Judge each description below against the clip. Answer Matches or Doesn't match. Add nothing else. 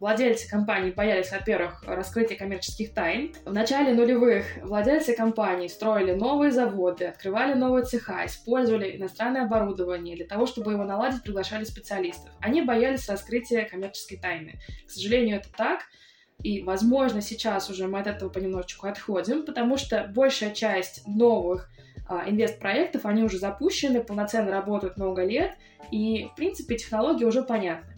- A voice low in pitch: Doesn't match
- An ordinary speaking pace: Matches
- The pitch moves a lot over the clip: Doesn't match